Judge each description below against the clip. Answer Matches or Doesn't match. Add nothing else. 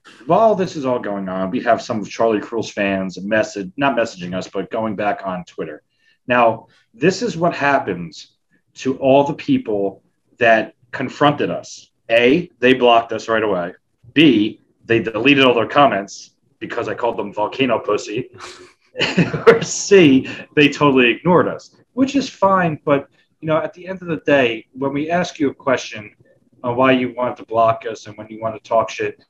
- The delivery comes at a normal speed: Matches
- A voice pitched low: Matches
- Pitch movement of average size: Doesn't match